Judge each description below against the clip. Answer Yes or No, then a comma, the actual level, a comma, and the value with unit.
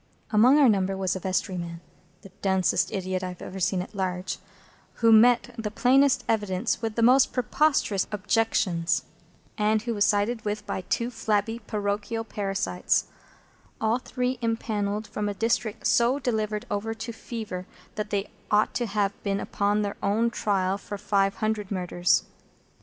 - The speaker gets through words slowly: No, average, 155 wpm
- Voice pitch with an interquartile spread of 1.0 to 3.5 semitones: Yes, average, 2.7 semitones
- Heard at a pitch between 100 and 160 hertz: No, high, 210 Hz